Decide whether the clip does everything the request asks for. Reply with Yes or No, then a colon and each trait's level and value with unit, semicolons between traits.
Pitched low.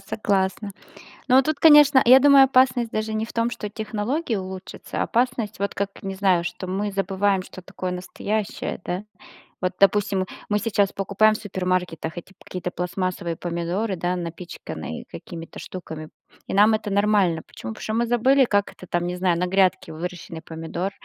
No: high, 195 Hz